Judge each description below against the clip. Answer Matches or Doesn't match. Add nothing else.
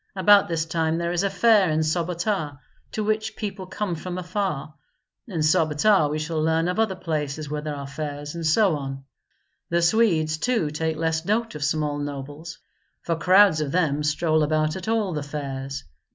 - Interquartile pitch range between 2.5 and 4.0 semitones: Matches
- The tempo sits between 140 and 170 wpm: Doesn't match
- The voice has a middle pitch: Matches